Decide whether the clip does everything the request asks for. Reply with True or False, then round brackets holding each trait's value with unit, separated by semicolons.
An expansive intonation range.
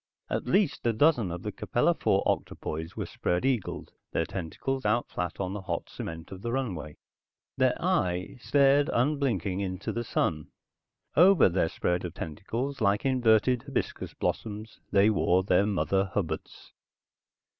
True (5.9 semitones)